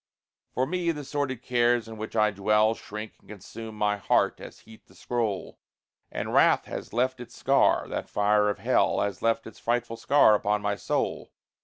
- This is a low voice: Yes, low, 110 Hz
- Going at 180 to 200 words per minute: Yes, average, 185 wpm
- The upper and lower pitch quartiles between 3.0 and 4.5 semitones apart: No, narrow, 2.6 semitones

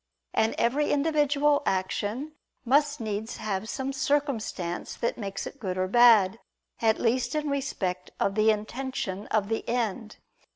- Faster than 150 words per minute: No, average, 140 wpm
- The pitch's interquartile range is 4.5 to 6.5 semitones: Yes, average, 5.3 semitones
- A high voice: Yes, high, 230 Hz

